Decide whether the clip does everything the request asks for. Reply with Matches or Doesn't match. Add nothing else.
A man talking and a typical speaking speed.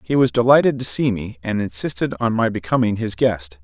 Doesn't match